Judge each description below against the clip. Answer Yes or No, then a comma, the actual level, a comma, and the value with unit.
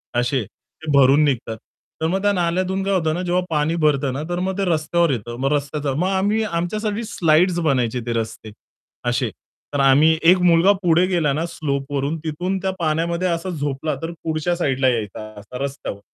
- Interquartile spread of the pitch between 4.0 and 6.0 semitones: Yes, average, 4.4 semitones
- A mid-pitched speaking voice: Yes, medium, 160 Hz